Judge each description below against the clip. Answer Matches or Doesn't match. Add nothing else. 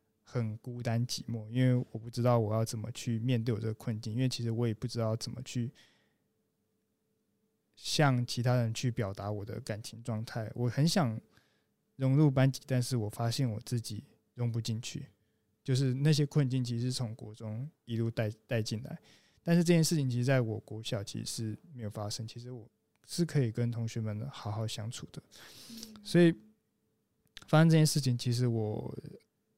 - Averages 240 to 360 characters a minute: Matches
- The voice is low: Matches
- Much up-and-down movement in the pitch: Doesn't match